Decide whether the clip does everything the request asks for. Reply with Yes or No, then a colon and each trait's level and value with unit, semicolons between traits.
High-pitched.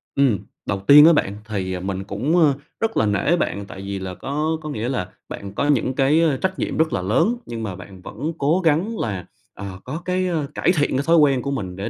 No: low, 135 Hz